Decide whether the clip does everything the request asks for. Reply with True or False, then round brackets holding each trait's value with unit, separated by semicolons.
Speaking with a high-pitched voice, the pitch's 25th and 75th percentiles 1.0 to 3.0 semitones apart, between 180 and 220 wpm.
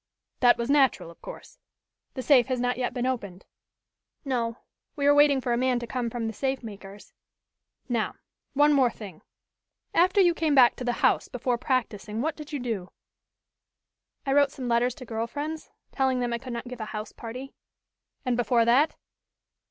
True (245 Hz; 2.7 semitones; 185 wpm)